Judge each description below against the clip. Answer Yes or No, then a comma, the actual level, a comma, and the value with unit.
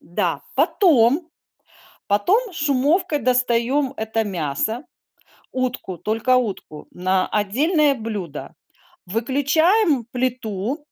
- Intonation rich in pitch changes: Yes, wide, 5.8 semitones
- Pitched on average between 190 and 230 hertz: No, very high, 250 Hz